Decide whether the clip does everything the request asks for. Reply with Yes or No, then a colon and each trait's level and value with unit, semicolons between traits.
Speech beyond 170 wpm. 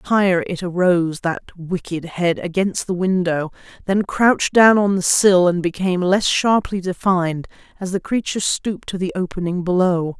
No: average, 155 wpm